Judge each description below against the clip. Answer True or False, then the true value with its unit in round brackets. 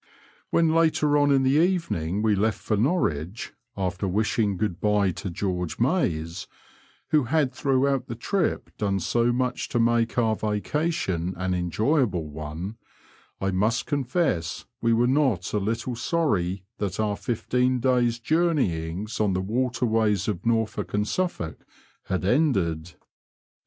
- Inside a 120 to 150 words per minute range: True (140 wpm)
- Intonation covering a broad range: True (5.8 semitones)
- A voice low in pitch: True (110 Hz)